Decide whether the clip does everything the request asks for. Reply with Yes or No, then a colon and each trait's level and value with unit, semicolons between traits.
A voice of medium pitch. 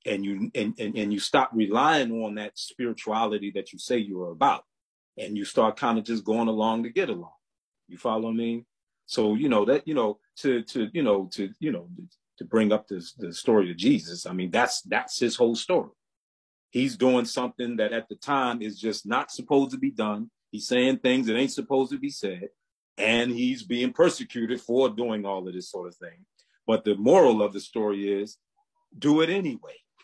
No: low, 115 Hz